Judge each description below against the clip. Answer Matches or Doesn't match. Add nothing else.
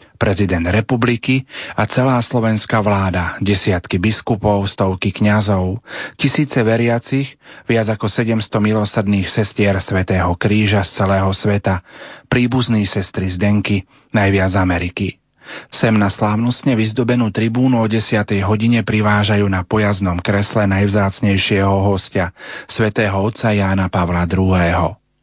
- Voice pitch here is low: Matches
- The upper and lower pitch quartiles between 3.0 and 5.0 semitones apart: Doesn't match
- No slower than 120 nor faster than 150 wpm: Doesn't match